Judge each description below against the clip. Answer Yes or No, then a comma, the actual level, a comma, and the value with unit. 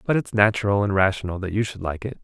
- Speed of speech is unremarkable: No, fast, 270 wpm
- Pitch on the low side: Yes, low, 100 Hz